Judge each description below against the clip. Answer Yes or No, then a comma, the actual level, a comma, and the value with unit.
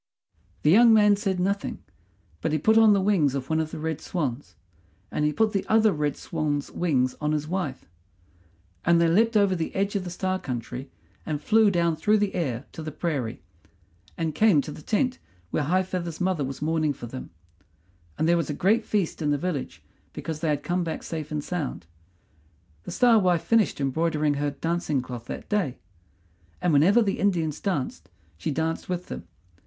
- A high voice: No, medium, 165 Hz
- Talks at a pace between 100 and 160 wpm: No, average, 195 wpm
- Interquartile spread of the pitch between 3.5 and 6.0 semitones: Yes, average, 4.7 semitones